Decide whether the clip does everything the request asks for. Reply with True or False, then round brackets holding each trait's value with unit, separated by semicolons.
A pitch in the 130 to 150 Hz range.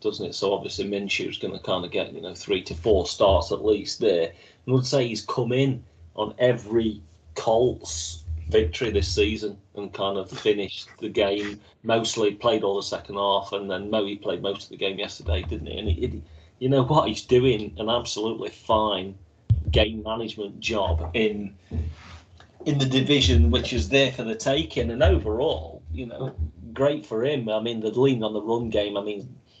False (105 Hz)